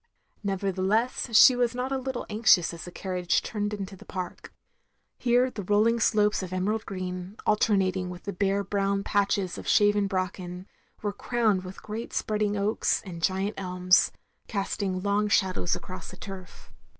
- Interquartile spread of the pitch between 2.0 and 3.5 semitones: Yes, narrow, 2.4 semitones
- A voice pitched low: No, high, 200 Hz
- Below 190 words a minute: Yes, average, 165 wpm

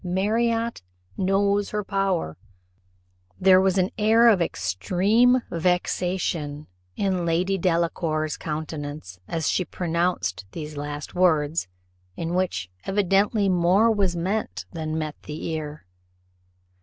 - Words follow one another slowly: Yes, slow, 110 wpm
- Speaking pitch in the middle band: Yes, medium, 180 Hz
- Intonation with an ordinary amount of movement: Yes, average, 4.0 semitones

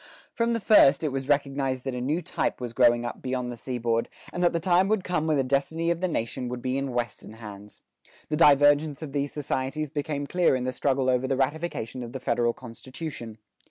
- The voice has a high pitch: No, low, 135 Hz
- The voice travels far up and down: No, average, 3.7 semitones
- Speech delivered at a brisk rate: Yes, fast, 220 wpm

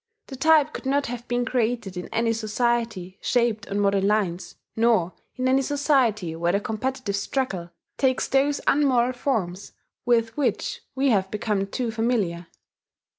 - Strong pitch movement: No, average, 4.5 semitones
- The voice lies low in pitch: No, high, 230 Hz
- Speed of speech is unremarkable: Yes, average, 150 wpm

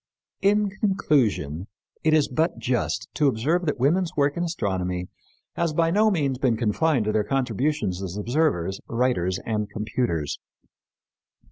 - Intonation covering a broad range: Yes, wide, 7.5 semitones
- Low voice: Yes, low, 130 Hz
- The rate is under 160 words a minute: Yes, average, 140 wpm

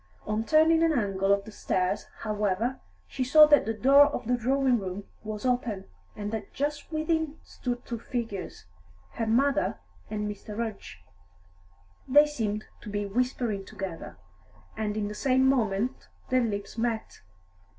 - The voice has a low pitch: No, high, 225 Hz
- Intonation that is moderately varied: Yes, average, 4.2 semitones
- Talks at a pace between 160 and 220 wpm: No, average, 150 wpm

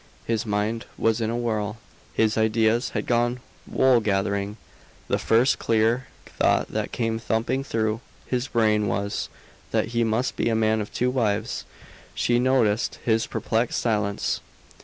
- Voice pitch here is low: Yes, low, 115 Hz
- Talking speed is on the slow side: No, average, 150 wpm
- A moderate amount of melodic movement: No, narrow, 1.8 semitones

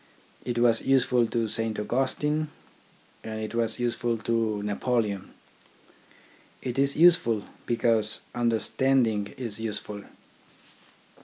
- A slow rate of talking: Yes, slow, 100 wpm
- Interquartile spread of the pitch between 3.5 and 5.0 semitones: No, narrow, 2.4 semitones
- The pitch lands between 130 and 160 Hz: No, low, 115 Hz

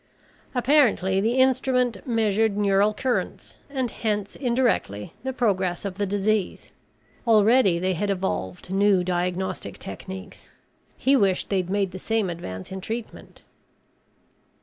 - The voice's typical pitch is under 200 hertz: No, high, 205 Hz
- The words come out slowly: Yes, slow, 125 wpm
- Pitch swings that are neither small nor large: Yes, average, 4.0 semitones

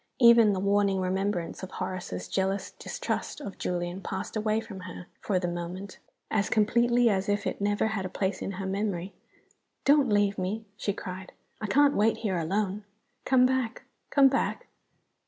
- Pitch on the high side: Yes, high, 200 Hz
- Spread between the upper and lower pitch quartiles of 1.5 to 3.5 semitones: Yes, average, 2.7 semitones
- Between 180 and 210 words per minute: No, average, 170 wpm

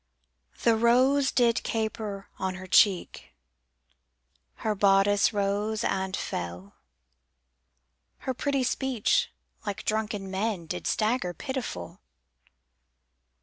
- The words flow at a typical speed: No, slow, 95 wpm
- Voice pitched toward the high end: Yes, high, 210 Hz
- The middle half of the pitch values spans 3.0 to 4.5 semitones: Yes, average, 3.6 semitones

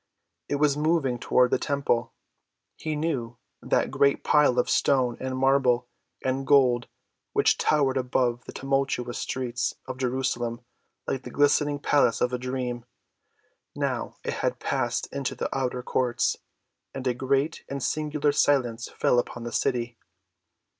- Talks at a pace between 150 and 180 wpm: No, average, 140 wpm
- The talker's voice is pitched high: No, low, 130 Hz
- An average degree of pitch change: No, narrow, 2.3 semitones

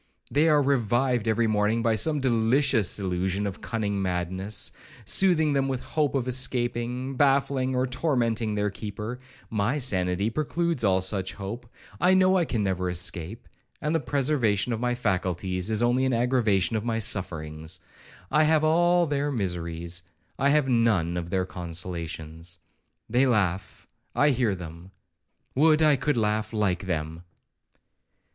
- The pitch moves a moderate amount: No, wide, 6.2 semitones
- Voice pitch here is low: Yes, low, 110 Hz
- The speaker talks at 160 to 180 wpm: No, average, 145 wpm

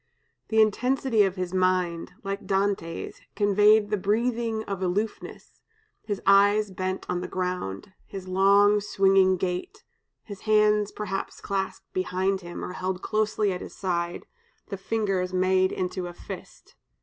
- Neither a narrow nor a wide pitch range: No, narrow, 2.2 semitones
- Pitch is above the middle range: Yes, high, 195 Hz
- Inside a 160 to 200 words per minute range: No, average, 140 wpm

